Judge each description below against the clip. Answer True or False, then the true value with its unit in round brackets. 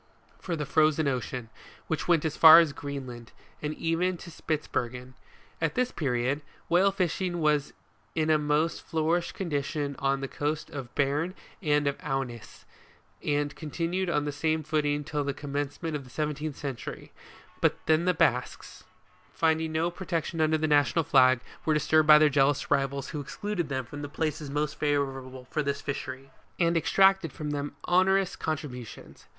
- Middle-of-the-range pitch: True (150 Hz)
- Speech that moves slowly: False (165 wpm)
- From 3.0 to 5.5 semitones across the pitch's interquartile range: False (2.6 semitones)